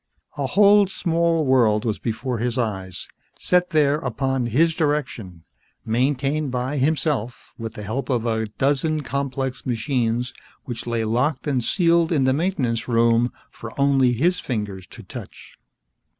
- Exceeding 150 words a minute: No, average, 145 wpm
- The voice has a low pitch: Yes, low, 130 Hz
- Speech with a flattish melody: No, average, 4.4 semitones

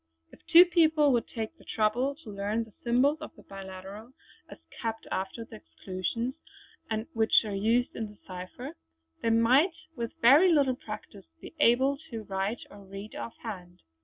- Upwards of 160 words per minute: Yes, average, 170 wpm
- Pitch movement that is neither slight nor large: Yes, average, 4.4 semitones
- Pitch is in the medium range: No, high, 225 Hz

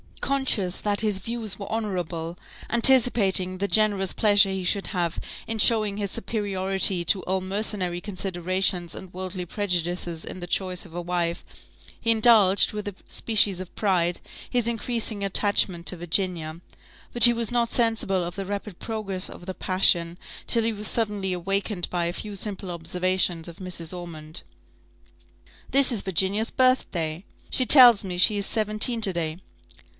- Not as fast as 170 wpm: Yes, average, 160 wpm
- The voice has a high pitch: Yes, high, 195 Hz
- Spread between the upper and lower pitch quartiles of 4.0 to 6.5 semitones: No, average, 3.2 semitones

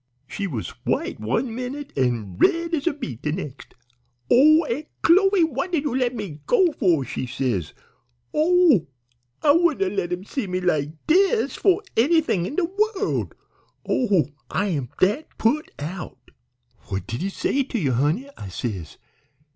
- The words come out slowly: No, average, 165 wpm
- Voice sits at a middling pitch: No, high, 225 Hz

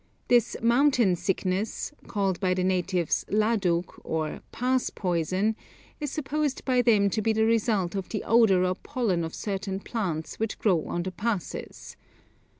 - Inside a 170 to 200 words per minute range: No, average, 150 wpm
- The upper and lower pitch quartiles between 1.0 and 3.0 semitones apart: No, average, 4.1 semitones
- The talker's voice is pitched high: Yes, high, 200 Hz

